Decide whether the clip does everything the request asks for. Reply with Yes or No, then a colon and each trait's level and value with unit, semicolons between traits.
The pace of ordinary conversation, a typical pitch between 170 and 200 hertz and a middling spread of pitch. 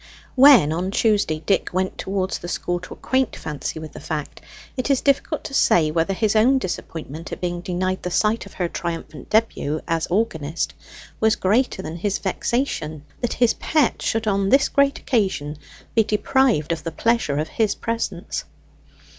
No: average, 170 wpm; high, 190 Hz; wide, 5.8 semitones